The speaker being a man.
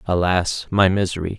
Yes: male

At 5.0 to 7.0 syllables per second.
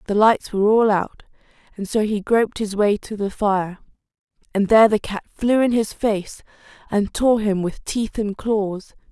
No: 4.6 syllables/s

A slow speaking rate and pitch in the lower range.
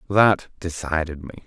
Yes: slow, 125 wpm; very low, 85 Hz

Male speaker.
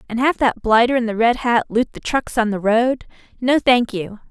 No: female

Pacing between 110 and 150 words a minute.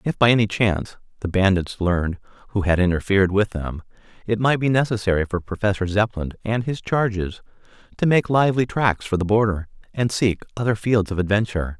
No: average, 180 wpm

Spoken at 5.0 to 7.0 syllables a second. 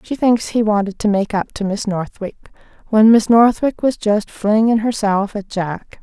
No: 4.5 syllables/s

